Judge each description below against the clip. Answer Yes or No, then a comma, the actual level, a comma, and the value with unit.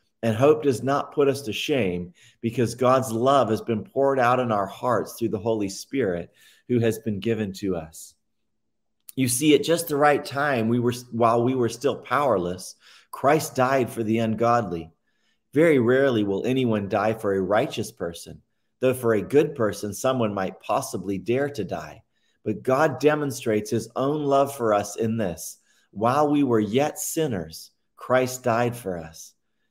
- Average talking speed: Yes, average, 175 wpm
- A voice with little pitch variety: No, average, 3.5 semitones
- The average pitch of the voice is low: Yes, low, 115 Hz